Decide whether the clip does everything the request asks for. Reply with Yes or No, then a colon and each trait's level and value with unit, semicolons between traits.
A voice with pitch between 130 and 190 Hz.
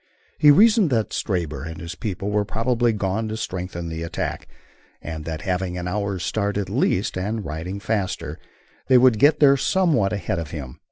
No: low, 100 Hz